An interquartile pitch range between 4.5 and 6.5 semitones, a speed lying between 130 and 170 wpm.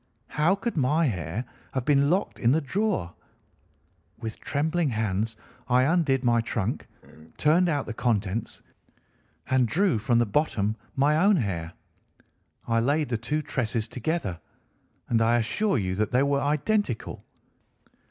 Yes: wide, 5.4 semitones; average, 145 wpm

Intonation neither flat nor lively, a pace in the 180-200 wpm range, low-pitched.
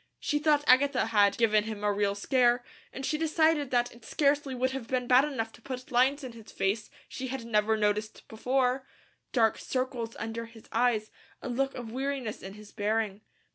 No: average, 3.5 semitones; average, 190 wpm; high, 245 Hz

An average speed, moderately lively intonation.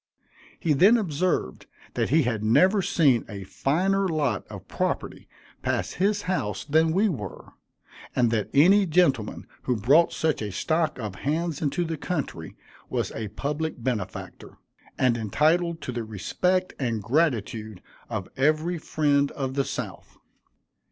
No: average, 145 wpm; wide, 6.6 semitones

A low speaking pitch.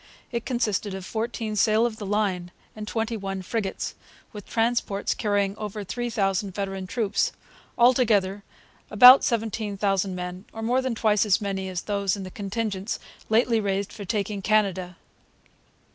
No: high, 205 Hz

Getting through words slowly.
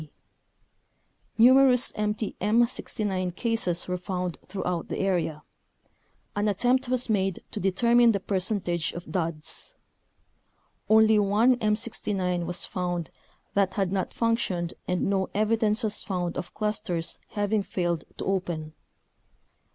Yes: slow, 120 wpm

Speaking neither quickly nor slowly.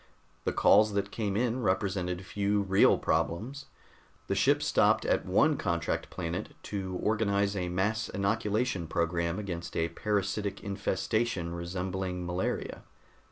No: slow, 125 wpm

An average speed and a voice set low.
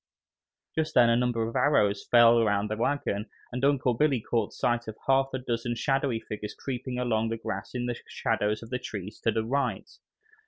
Yes: average, 195 wpm; low, 120 Hz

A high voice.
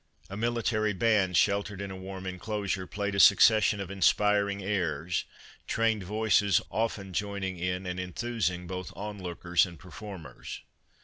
No: low, 100 Hz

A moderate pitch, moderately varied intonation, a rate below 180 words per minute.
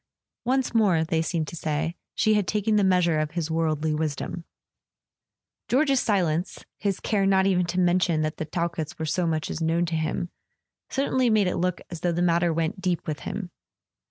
No: medium, 175 Hz; average, 3.3 semitones; average, 185 wpm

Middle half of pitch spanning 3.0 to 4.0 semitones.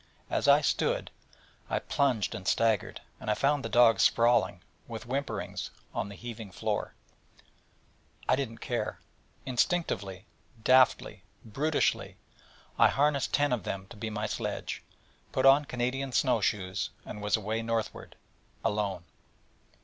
No: average, 4.4 semitones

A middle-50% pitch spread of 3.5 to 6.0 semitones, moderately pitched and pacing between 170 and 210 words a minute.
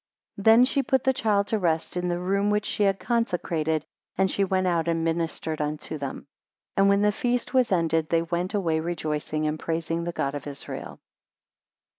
Yes: average, 4.0 semitones; medium, 175 Hz; average, 200 wpm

